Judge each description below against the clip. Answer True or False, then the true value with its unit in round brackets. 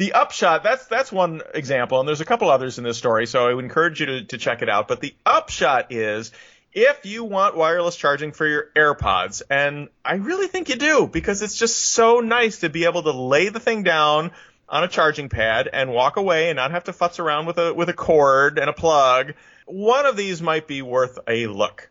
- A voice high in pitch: False (160 Hz)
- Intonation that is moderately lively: False (6.4 semitones)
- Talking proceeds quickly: True (230 wpm)